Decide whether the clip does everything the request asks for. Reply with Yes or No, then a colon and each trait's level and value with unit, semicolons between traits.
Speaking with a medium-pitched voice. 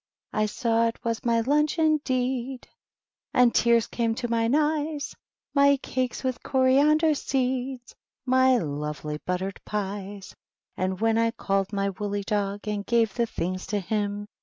No: high, 230 Hz